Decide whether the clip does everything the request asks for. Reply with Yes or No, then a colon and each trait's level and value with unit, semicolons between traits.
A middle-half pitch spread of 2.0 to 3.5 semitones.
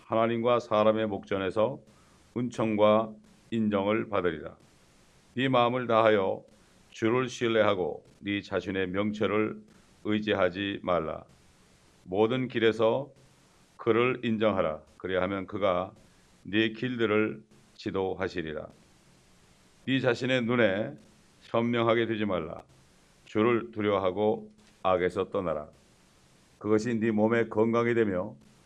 Yes: average, 2.7 semitones